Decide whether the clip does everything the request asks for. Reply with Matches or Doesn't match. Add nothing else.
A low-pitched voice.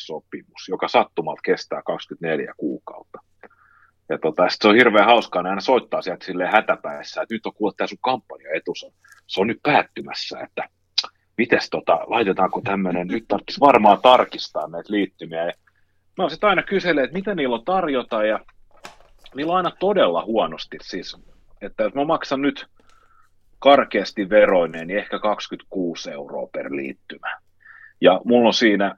Matches